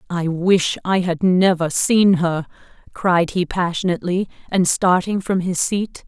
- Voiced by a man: No, female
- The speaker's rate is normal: Yes, average, 150 wpm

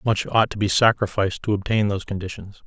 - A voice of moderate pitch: No, low, 100 Hz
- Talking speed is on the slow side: No, fast, 205 wpm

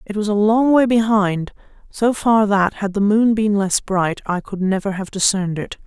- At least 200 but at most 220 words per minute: Yes, fast, 205 wpm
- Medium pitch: No, high, 205 Hz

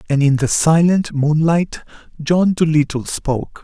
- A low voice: No, medium, 155 Hz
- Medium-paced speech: No, slow, 130 wpm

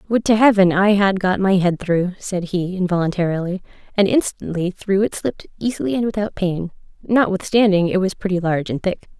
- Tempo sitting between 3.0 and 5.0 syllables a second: No, 5.5 syllables/s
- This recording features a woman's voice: Yes, female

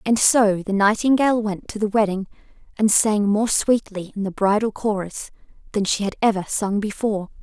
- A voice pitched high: Yes, high, 210 Hz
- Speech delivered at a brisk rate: No, average, 180 wpm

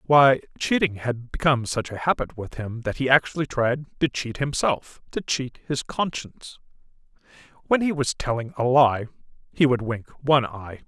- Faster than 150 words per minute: Yes, average, 165 wpm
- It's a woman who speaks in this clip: No, male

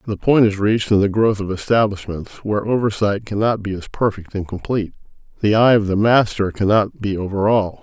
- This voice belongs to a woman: No, male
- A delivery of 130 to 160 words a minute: No, average, 200 wpm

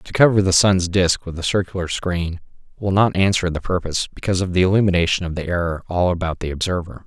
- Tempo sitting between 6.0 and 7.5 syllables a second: Yes, 6.1 syllables/s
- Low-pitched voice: Yes, very low, 90 Hz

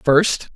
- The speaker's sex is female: No, male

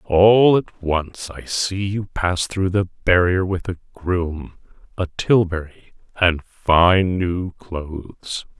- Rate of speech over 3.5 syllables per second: No, 3.1 syllables/s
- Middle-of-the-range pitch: No, very low, 90 Hz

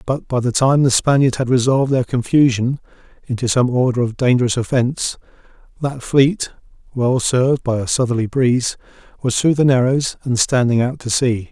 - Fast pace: No, average, 170 wpm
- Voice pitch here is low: Yes, low, 125 Hz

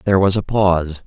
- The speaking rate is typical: No, fast, 225 wpm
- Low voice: Yes, very low, 95 Hz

